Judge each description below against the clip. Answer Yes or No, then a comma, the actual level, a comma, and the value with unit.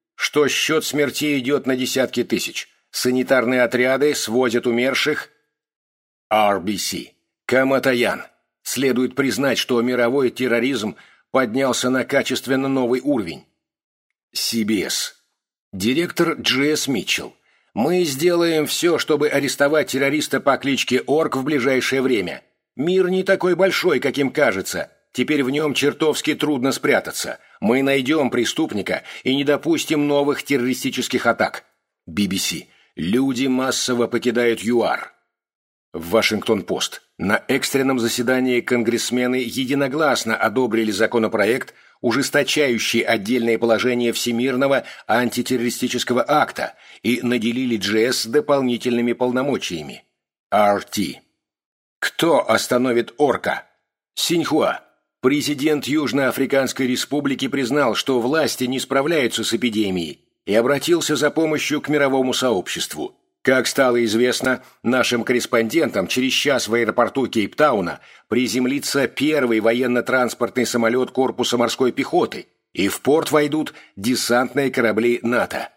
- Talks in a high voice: No, low, 130 Hz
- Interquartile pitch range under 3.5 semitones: Yes, average, 2.8 semitones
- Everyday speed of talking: No, slow, 105 wpm